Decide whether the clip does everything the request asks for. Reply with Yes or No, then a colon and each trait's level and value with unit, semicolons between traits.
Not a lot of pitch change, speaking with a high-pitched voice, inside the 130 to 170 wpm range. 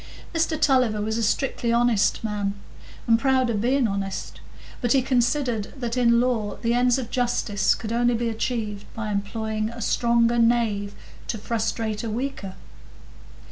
Yes: narrow, 2.3 semitones; high, 230 Hz; average, 155 wpm